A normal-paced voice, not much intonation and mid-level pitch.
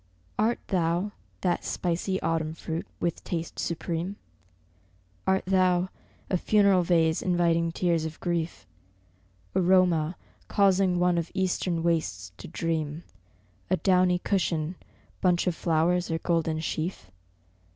No: slow, 120 wpm; narrow, 2.1 semitones; medium, 175 Hz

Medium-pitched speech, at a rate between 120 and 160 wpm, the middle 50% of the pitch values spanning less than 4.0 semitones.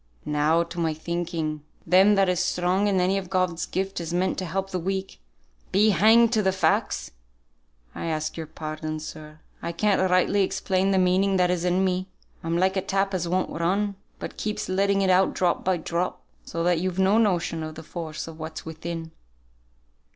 No: medium, 180 Hz; average, 195 wpm; narrow, 2.5 semitones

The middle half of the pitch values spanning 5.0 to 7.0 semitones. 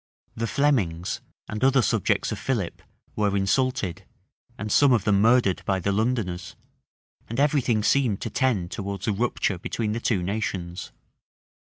No: average, 4.2 semitones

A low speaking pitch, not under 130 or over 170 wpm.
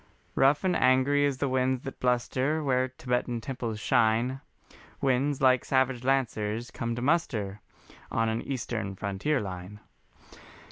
Yes: low, 130 Hz; slow, 135 wpm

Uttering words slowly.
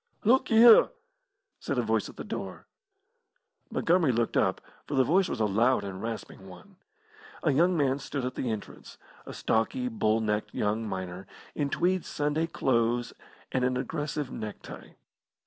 No: average, 165 wpm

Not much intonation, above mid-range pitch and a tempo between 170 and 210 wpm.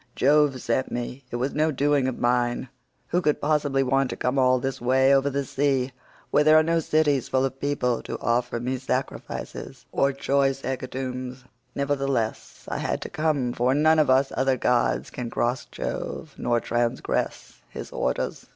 No: narrow, 2.2 semitones; low, 135 Hz; average, 175 wpm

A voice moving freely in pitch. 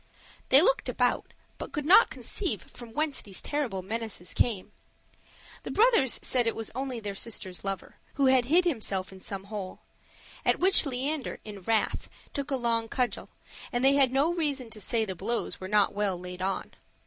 Yes: wide, 5.7 semitones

